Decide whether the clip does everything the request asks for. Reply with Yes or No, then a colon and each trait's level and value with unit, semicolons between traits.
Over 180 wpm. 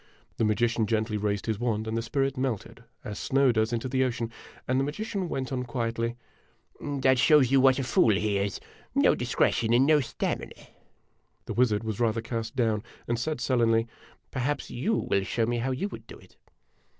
Yes: average, 195 wpm